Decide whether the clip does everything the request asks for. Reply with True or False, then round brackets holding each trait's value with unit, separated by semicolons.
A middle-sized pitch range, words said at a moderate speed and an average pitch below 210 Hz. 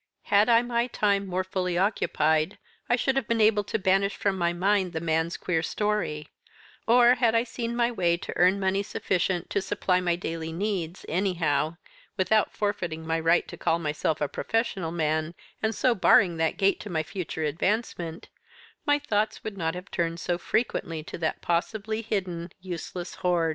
True (4.2 semitones; 180 wpm; 185 Hz)